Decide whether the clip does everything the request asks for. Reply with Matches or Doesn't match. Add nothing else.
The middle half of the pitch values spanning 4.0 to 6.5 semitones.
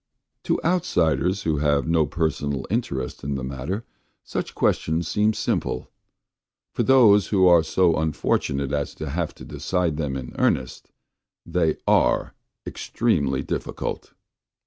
Matches